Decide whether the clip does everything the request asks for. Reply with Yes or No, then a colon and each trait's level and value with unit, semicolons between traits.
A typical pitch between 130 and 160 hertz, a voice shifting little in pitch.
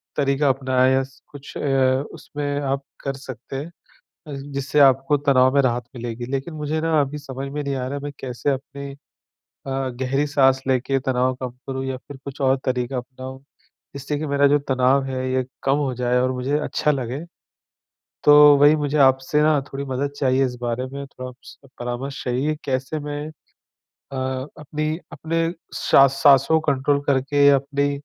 Yes: low, 135 Hz; narrow, 1.8 semitones